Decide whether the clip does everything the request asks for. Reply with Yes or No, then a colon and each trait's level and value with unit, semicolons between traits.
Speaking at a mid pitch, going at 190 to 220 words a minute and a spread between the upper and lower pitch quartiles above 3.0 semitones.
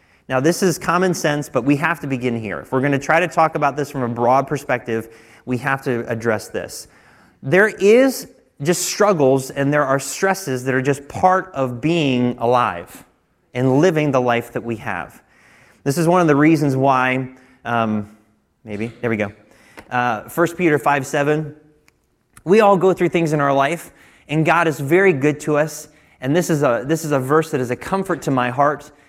Yes: medium, 145 Hz; average, 200 wpm; average, 4.4 semitones